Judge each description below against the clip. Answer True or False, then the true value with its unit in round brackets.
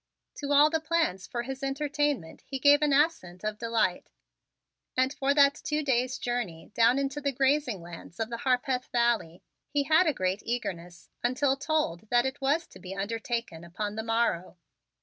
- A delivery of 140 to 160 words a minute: False (175 wpm)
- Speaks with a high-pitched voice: True (250 Hz)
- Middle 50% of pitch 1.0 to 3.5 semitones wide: False (5.1 semitones)